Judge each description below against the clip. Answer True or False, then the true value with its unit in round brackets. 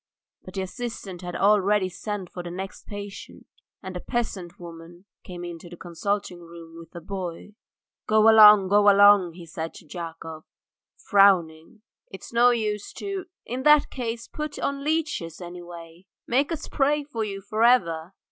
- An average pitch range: True (4.4 semitones)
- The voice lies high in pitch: True (195 Hz)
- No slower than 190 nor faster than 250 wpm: False (165 wpm)